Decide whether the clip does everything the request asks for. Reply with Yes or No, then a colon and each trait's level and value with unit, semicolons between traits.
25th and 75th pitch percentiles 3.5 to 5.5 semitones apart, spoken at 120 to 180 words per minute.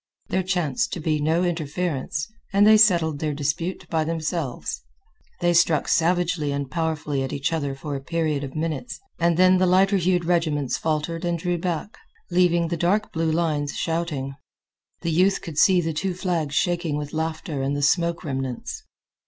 No: average, 3.0 semitones; average, 175 wpm